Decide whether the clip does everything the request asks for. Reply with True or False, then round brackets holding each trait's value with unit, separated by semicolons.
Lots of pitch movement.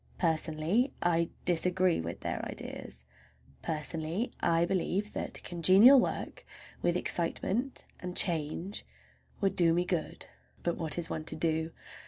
False (2.6 semitones)